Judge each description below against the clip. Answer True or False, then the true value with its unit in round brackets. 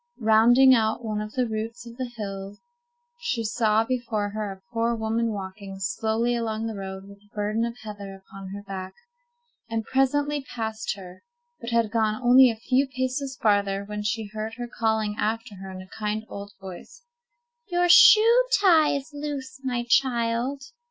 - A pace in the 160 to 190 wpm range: True (170 wpm)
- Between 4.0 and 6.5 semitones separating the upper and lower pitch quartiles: False (3.4 semitones)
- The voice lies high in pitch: True (225 Hz)